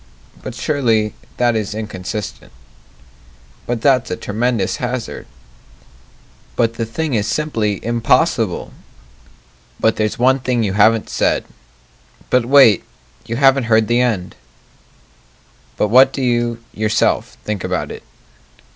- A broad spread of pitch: No, average, 2.8 semitones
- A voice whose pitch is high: No, low, 115 Hz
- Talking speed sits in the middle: No, slow, 120 wpm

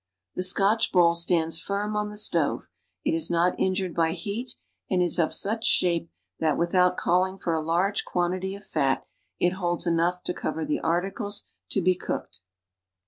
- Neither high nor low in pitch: Yes, medium, 180 Hz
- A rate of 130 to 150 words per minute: No, average, 175 wpm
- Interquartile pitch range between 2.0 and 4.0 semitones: Yes, average, 2.7 semitones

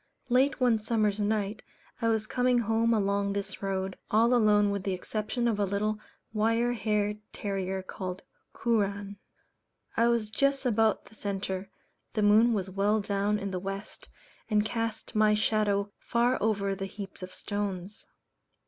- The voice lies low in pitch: No, high, 210 Hz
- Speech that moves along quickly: No, average, 155 wpm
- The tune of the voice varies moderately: No, narrow, 2.1 semitones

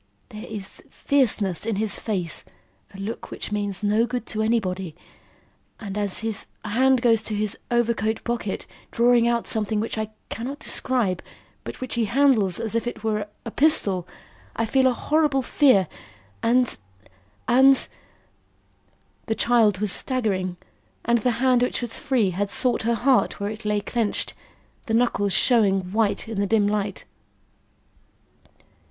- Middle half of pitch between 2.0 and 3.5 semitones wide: Yes, average, 2.9 semitones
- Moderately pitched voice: No, high, 220 Hz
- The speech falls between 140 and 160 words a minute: Yes, average, 155 wpm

